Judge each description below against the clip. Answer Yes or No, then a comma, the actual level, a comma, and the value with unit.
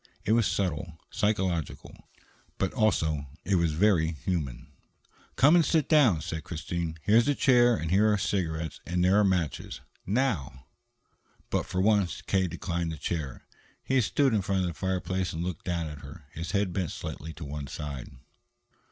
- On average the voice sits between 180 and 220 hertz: No, very low, 90 Hz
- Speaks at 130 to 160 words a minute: No, average, 170 wpm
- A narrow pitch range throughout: No, average, 4.5 semitones